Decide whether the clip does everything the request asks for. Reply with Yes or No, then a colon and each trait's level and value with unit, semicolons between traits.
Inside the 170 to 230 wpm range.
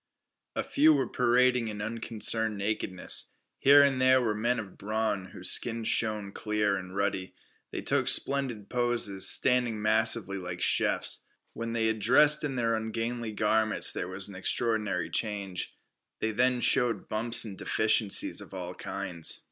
No: average, 155 wpm